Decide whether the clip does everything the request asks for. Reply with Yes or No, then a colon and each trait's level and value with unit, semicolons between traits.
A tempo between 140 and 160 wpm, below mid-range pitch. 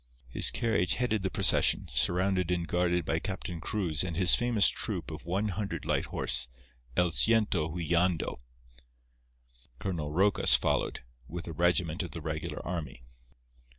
Yes: average, 145 wpm; very low, 90 Hz